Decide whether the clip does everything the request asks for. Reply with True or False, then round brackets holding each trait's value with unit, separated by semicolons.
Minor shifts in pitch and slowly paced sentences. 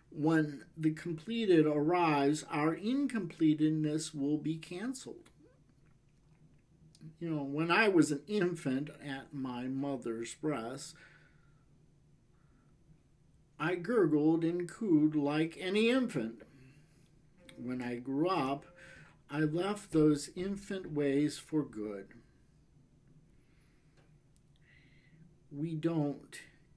True (2.2 semitones; 90 wpm)